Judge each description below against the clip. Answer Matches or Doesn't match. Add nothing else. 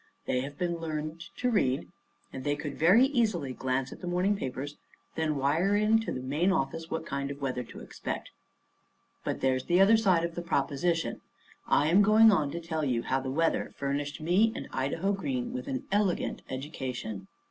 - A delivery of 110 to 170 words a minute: Doesn't match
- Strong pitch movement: Matches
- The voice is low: Doesn't match